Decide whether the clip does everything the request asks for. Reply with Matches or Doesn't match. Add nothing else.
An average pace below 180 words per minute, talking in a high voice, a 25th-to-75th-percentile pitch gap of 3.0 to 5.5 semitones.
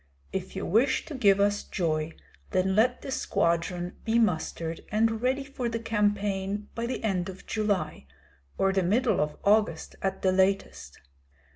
Matches